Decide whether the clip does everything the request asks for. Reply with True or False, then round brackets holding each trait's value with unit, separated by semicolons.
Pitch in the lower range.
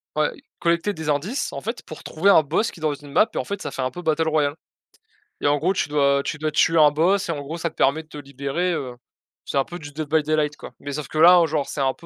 False (155 Hz)